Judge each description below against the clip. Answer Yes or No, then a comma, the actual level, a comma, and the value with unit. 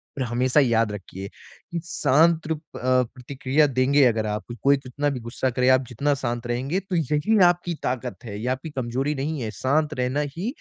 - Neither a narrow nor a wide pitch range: Yes, average, 3.6 semitones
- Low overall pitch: Yes, low, 130 Hz